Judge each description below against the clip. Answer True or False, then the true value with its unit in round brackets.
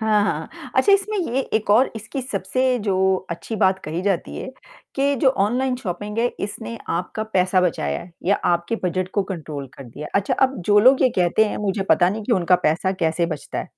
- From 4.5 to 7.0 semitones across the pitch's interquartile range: True (4.9 semitones)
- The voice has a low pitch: False (200 Hz)